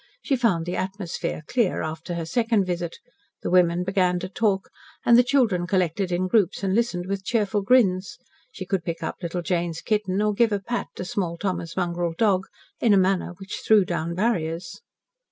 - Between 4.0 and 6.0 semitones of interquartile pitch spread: No, average, 3.1 semitones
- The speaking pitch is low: No, medium, 185 Hz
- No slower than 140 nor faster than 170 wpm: No, average, 190 wpm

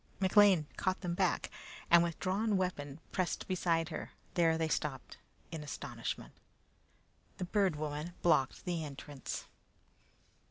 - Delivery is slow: Yes, slow, 125 wpm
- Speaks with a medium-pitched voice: Yes, medium, 170 Hz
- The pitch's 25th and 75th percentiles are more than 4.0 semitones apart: No, average, 3.6 semitones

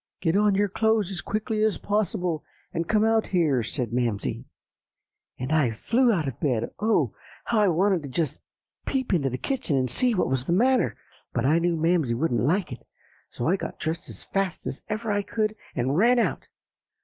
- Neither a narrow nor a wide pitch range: No, wide, 7.5 semitones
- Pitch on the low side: No, medium, 175 Hz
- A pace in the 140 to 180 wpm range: No, average, 195 wpm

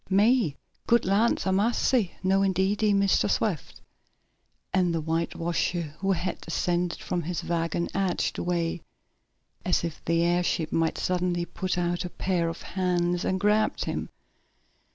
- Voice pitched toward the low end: No, medium, 180 Hz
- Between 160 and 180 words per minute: No, average, 140 wpm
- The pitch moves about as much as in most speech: No, narrow, 2.1 semitones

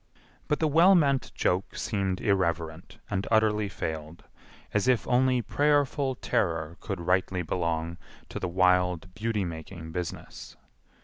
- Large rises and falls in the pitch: Yes, wide, 6.0 semitones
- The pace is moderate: No, slow, 130 wpm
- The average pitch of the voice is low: Yes, very low, 95 Hz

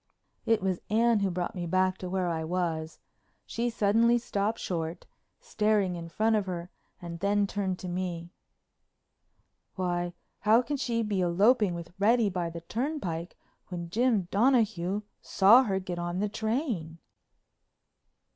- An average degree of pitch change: Yes, average, 4.0 semitones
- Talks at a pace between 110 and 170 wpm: Yes, average, 145 wpm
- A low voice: No, high, 190 Hz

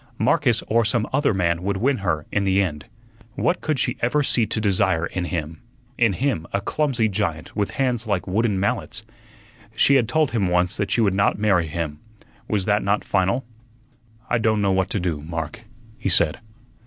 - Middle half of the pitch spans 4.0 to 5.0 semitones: Yes, average, 4.7 semitones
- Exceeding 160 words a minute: Yes, average, 190 wpm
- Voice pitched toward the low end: Yes, low, 100 Hz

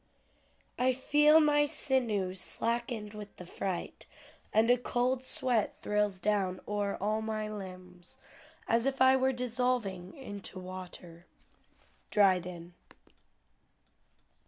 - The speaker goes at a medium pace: No, slow, 110 wpm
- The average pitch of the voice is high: Yes, high, 210 Hz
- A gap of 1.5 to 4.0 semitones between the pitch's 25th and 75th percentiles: No, average, 5.1 semitones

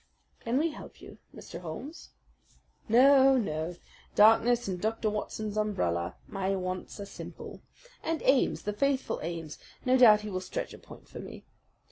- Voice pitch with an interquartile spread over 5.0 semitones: Yes, wide, 5.5 semitones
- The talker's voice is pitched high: Yes, high, 215 Hz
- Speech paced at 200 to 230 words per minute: No, average, 155 wpm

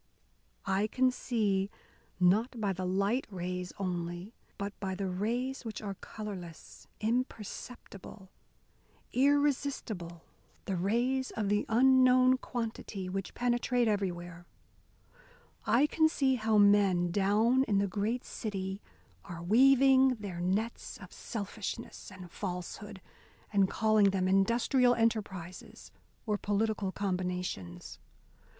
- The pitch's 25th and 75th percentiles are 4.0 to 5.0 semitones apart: Yes, average, 4.3 semitones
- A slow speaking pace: Yes, slow, 110 wpm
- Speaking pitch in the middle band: No, high, 205 Hz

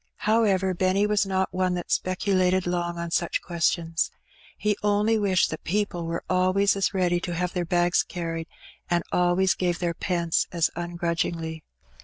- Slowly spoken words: No, average, 165 wpm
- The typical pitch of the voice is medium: Yes, medium, 180 Hz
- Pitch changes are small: Yes, narrow, 1.8 semitones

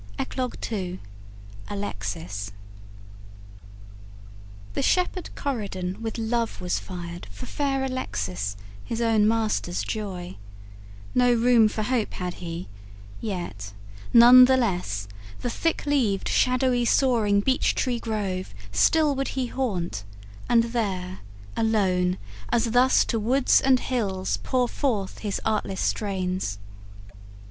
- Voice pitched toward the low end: No, high, 215 Hz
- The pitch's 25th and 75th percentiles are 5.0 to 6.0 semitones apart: Yes, wide, 5.4 semitones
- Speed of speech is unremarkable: No, slow, 115 wpm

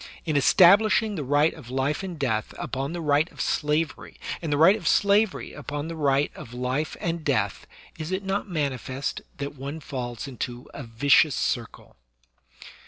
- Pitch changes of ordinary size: Yes, average, 3.8 semitones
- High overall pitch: No, medium, 145 Hz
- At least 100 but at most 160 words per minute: No, average, 170 wpm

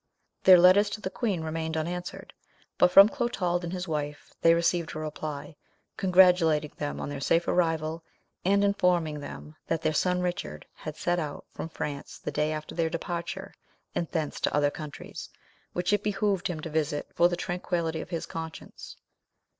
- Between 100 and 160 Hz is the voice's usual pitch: No, medium, 170 Hz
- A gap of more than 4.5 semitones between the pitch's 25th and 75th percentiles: No, narrow, 2.5 semitones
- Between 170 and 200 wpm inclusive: Yes, average, 175 wpm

